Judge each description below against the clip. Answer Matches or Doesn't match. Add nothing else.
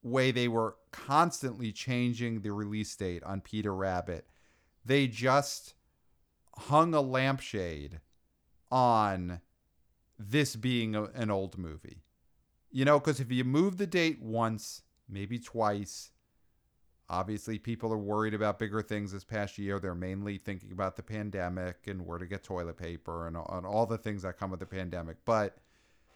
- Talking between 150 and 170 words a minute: Matches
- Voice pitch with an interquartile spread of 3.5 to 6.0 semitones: Matches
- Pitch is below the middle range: Matches